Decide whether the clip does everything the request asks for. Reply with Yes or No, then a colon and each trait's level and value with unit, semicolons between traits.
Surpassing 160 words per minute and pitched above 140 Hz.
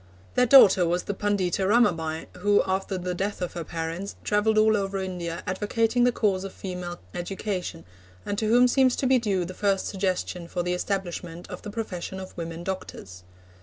Yes: average, 185 wpm; high, 190 Hz